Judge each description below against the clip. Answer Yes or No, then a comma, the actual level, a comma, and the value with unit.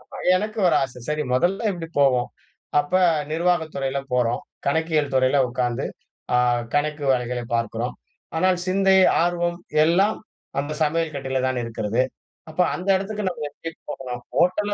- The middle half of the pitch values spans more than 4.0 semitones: Yes, wide, 5.6 semitones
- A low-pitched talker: No, medium, 150 Hz